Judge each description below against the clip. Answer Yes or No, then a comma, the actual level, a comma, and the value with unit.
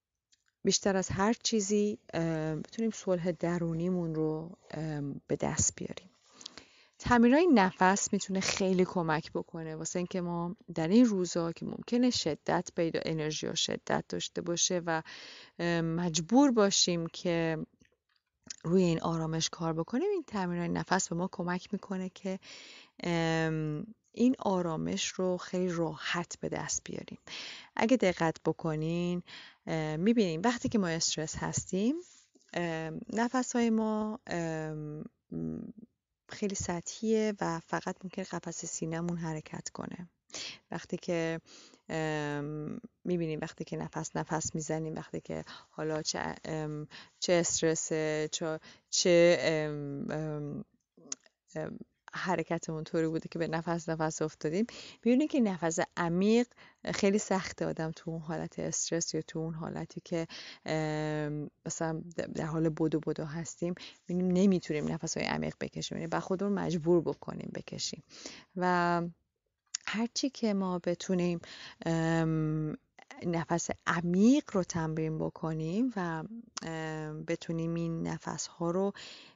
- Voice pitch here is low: No, medium, 170 Hz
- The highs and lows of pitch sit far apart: No, average, 3.2 semitones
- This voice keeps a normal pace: Yes, average, 115 wpm